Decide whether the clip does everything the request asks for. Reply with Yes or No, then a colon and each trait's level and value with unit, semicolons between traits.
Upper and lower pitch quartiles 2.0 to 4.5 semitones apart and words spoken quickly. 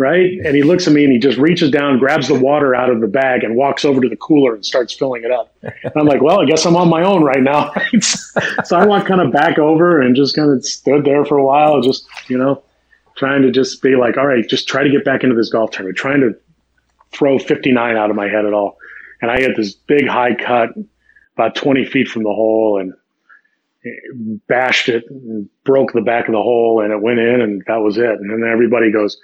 Yes: average, 4.1 semitones; fast, 250 wpm